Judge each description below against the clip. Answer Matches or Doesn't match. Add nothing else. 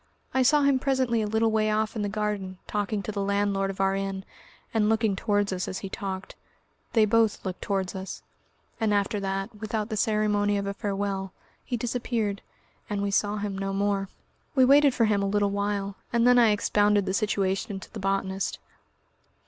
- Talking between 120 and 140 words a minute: Doesn't match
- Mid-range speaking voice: Doesn't match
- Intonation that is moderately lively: Doesn't match